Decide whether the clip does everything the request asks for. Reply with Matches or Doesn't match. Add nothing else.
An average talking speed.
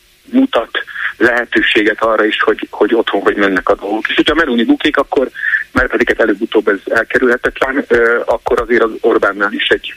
Doesn't match